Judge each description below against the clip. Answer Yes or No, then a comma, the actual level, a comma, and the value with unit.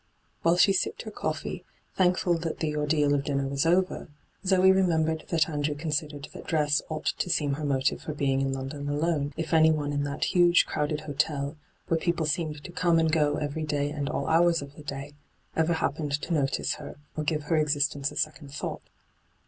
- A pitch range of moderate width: No, narrow, 2.1 semitones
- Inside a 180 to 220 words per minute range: Yes, average, 200 wpm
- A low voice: No, medium, 150 Hz